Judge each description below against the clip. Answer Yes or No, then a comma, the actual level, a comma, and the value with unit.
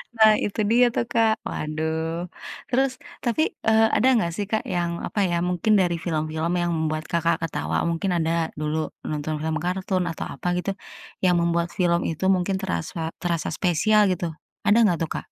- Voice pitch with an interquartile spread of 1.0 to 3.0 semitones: No, average, 3.6 semitones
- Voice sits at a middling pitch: Yes, medium, 170 Hz